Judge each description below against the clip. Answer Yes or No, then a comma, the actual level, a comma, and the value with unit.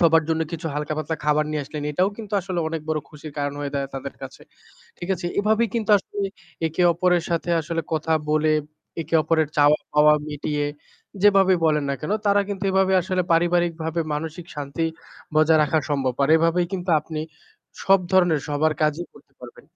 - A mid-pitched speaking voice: Yes, medium, 160 Hz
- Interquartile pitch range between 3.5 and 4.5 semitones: No, average, 3.0 semitones